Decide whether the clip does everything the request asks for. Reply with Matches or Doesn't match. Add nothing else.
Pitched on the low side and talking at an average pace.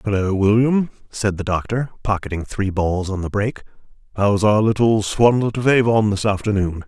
Matches